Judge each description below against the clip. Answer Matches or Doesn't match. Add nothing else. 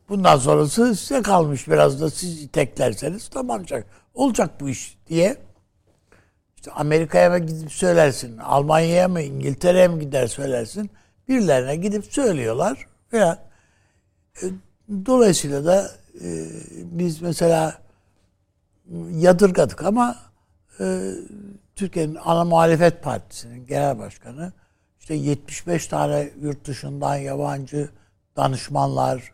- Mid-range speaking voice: Matches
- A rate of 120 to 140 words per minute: Doesn't match